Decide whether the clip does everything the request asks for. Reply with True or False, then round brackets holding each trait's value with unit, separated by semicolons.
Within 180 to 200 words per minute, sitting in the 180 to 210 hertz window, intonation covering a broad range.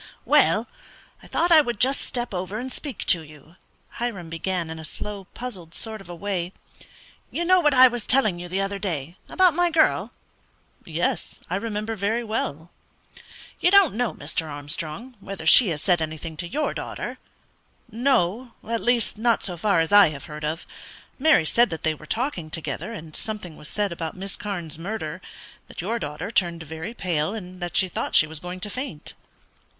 True (190 wpm; 190 Hz; 6.2 semitones)